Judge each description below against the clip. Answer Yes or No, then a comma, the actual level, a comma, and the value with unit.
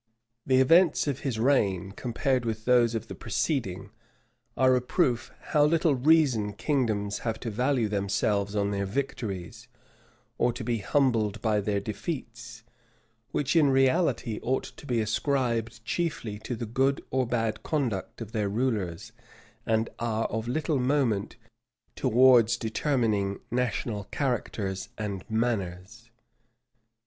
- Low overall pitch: Yes, low, 115 Hz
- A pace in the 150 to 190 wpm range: No, slow, 135 wpm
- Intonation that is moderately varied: Yes, average, 3.7 semitones